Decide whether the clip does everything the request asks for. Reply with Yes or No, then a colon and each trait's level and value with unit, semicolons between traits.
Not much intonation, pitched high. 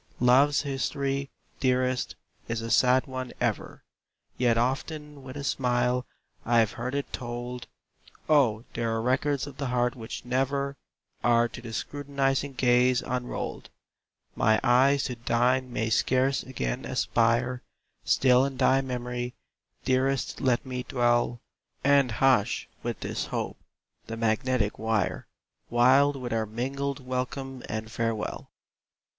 No: narrow, 2.1 semitones; low, 125 Hz